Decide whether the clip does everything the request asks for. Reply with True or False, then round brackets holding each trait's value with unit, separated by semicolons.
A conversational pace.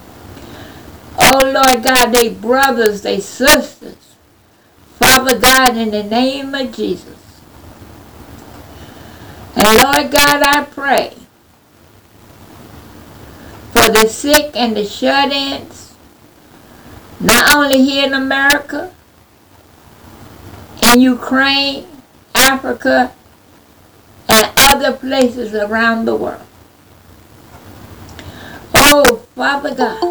False (85 wpm)